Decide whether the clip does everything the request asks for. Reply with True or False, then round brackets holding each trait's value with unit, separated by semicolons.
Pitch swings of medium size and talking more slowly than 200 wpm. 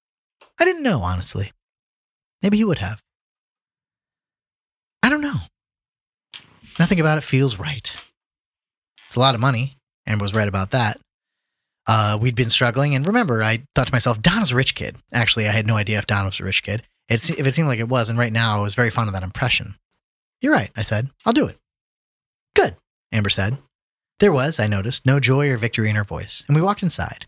False (5.0 semitones; 205 wpm)